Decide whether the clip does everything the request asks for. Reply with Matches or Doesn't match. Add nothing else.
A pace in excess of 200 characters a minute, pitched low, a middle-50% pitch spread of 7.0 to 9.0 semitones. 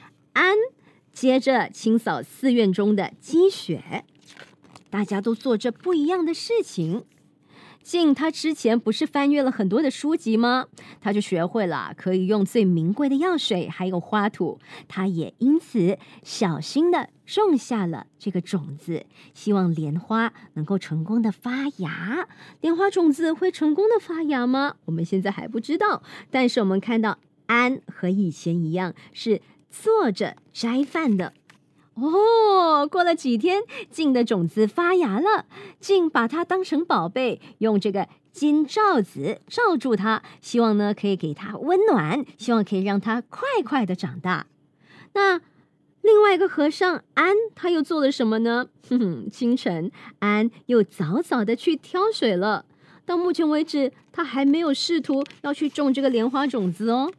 Doesn't match